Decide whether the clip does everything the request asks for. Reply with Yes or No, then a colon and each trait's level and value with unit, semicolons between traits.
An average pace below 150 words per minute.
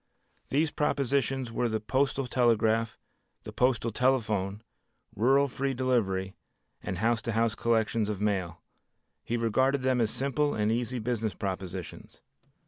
Yes: slow, 135 wpm